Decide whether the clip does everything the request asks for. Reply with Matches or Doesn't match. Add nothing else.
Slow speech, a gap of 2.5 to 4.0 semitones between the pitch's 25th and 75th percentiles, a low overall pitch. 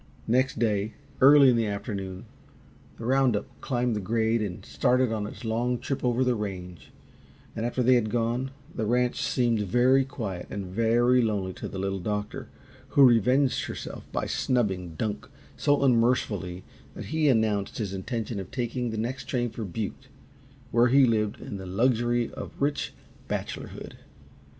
Doesn't match